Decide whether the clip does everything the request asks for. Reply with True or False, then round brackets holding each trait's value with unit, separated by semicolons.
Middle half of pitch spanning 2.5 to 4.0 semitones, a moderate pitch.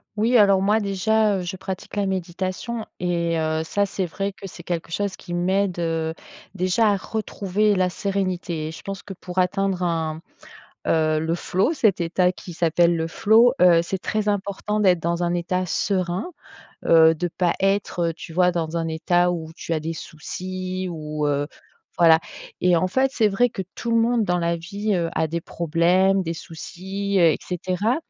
True (2.9 semitones; 180 Hz)